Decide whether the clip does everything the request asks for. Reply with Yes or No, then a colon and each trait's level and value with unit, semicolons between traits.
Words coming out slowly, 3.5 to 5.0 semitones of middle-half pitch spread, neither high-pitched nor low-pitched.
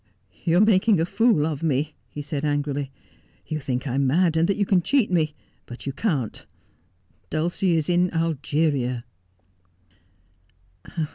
No: average, 160 wpm; average, 3.9 semitones; medium, 155 Hz